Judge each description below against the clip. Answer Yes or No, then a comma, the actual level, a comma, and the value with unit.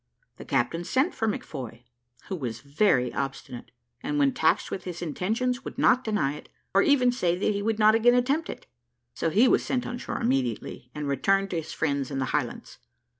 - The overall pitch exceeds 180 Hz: Yes, high, 190 Hz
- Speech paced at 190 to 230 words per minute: Yes, average, 200 wpm